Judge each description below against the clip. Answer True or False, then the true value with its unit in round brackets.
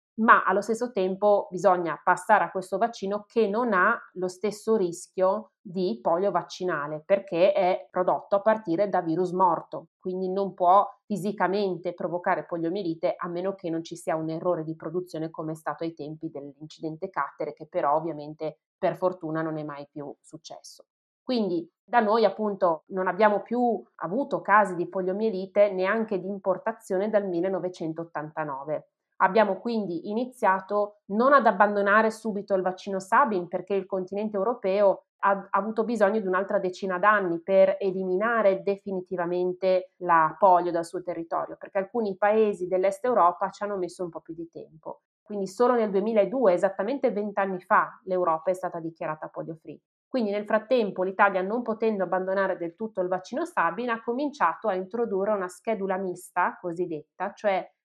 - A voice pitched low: False (190 Hz)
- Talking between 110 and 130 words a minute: False (160 wpm)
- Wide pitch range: False (2.8 semitones)